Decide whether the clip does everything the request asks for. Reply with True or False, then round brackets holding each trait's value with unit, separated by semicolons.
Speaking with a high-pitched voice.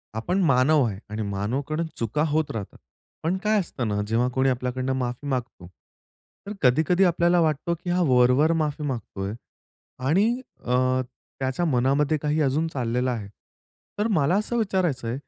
False (135 Hz)